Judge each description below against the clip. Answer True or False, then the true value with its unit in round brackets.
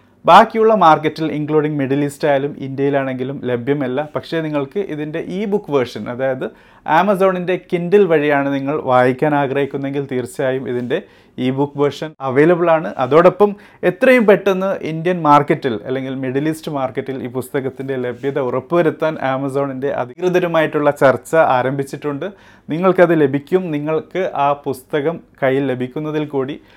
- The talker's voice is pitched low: False (145 Hz)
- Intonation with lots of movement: False (3.6 semitones)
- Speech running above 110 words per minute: True (120 wpm)